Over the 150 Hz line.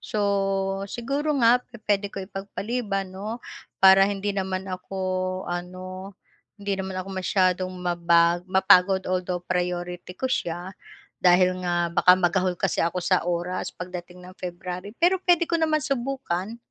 Yes: medium, 185 Hz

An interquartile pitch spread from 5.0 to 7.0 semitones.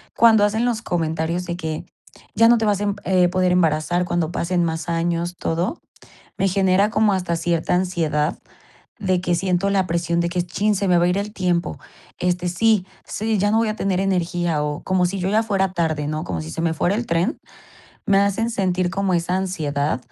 No: average, 2.8 semitones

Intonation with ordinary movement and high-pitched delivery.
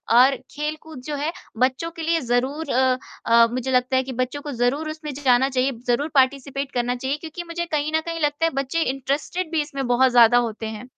Yes: average, 3.5 semitones; very high, 275 Hz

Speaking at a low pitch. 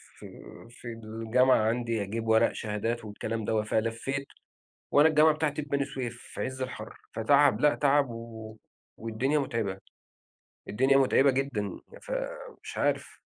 Yes: low, 120 Hz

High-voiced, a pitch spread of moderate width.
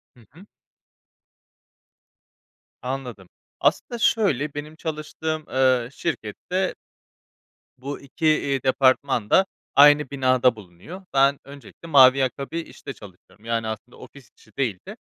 No: low, 135 Hz; average, 3.7 semitones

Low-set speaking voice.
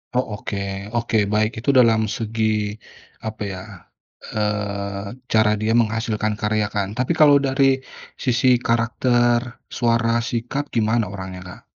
Yes: low, 110 Hz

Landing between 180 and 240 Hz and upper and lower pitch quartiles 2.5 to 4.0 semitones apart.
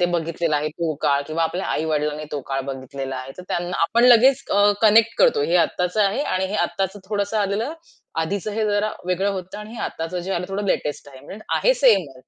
No: medium, 185 Hz; wide, 5.4 semitones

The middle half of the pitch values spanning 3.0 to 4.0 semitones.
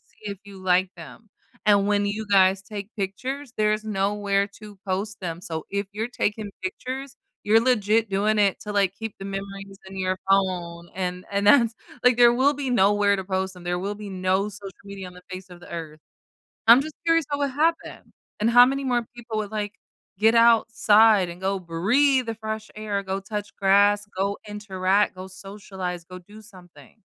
No: narrow, 2.5 semitones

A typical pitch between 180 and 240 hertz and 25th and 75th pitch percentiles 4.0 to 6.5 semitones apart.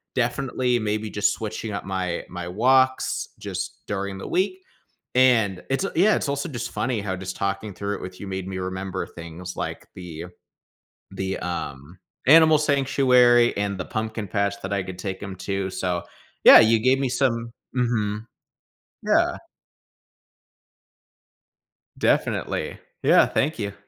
No: low, 105 Hz; average, 4.8 semitones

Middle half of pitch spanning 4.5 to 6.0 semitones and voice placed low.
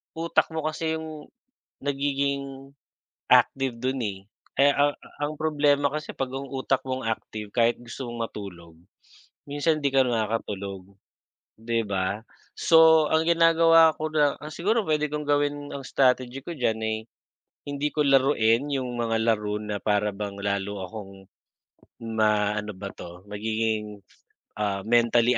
Yes: wide, 5.5 semitones; low, 130 Hz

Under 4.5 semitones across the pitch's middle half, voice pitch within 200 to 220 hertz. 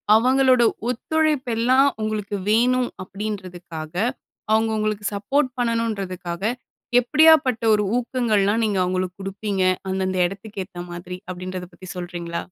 No: average, 4.8 semitones; high, 210 Hz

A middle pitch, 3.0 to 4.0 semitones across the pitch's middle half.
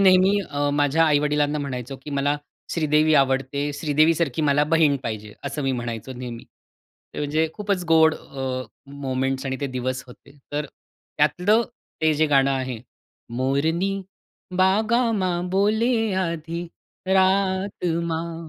No: medium, 150 Hz; average, 4.5 semitones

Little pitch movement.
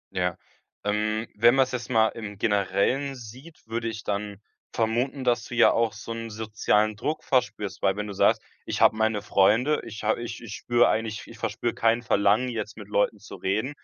Yes: narrow, 2.3 semitones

